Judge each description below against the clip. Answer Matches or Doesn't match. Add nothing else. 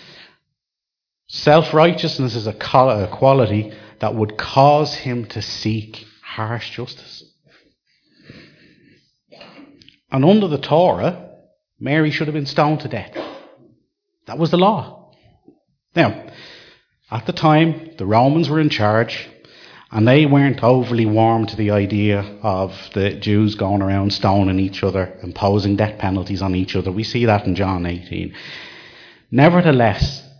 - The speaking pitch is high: Doesn't match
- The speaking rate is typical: Doesn't match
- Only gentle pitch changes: Doesn't match